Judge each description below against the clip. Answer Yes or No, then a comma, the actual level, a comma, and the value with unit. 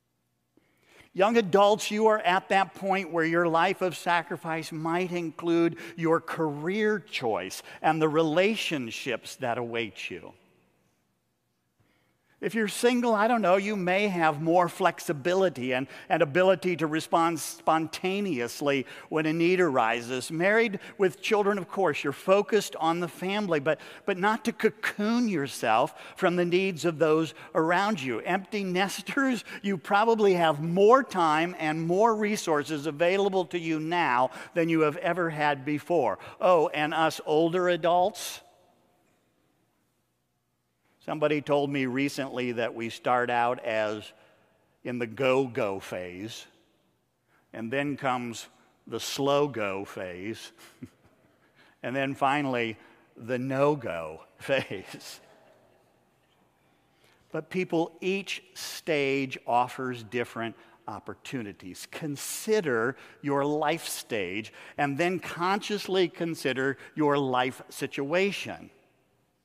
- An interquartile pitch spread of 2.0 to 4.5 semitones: No, wide, 5.4 semitones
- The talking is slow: Yes, slow, 120 wpm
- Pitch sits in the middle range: Yes, medium, 165 Hz